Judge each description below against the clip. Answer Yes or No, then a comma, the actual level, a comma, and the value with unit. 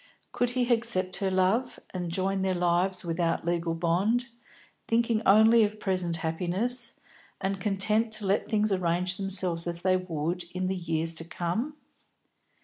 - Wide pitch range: No, average, 3.8 semitones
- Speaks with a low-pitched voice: No, medium, 185 Hz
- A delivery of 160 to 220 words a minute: No, average, 150 wpm